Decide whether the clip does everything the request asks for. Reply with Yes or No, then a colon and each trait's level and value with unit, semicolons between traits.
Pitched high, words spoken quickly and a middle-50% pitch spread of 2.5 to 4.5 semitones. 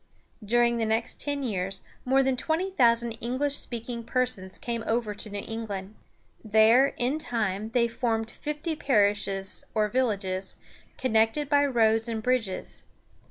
No: high, 230 Hz; average, 140 wpm; average, 3.0 semitones